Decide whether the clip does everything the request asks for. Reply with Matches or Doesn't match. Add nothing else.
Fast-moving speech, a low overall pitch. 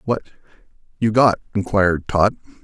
Doesn't match